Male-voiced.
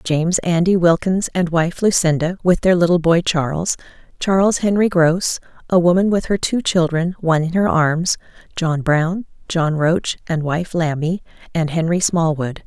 No: female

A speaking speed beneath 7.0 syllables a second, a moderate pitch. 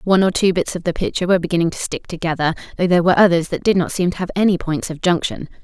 No: 7.5 syllables/s; medium, 175 Hz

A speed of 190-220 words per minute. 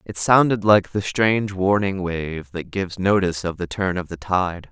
Yes: fast, 205 wpm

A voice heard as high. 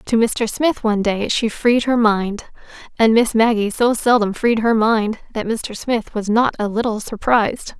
Yes: high, 220 Hz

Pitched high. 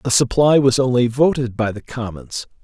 No: low, 125 Hz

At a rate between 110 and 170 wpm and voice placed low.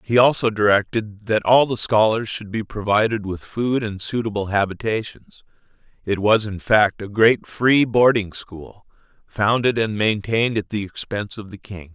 Yes: average, 165 wpm; low, 105 Hz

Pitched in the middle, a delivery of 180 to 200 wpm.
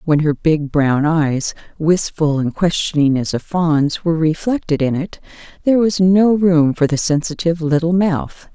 No: medium, 160 Hz; average, 170 wpm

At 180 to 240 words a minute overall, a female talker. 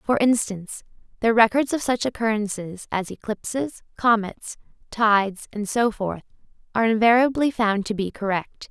No: average, 140 wpm; female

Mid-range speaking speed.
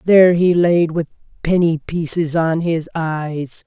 Yes: average, 145 wpm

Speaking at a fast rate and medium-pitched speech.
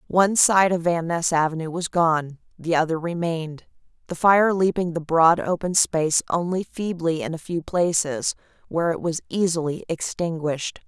No: average, 160 wpm; medium, 170 Hz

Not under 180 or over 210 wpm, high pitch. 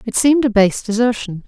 Yes: fast, 205 wpm; high, 230 Hz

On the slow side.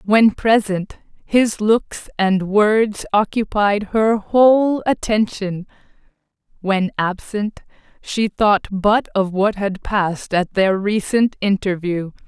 Yes: slow, 110 wpm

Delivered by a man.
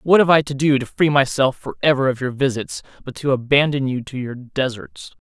Yes: male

